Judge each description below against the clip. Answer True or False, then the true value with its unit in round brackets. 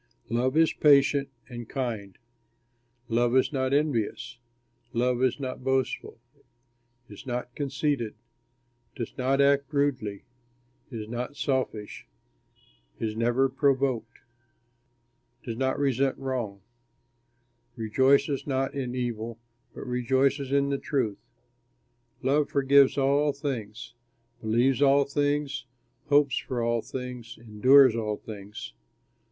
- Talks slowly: True (110 wpm)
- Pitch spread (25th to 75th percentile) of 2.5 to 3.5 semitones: True (2.8 semitones)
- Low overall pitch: True (130 Hz)